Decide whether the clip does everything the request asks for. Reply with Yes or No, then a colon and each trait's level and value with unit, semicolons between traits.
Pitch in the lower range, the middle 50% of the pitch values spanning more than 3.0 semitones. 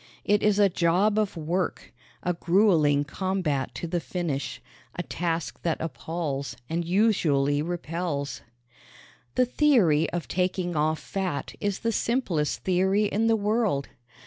No: medium, 175 Hz; average, 4.3 semitones